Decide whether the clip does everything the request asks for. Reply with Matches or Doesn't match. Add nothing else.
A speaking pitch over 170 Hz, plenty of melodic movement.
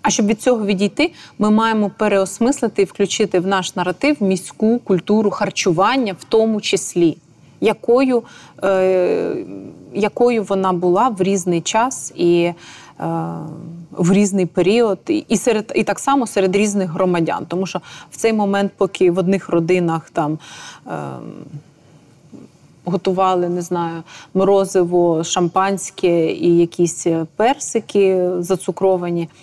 Doesn't match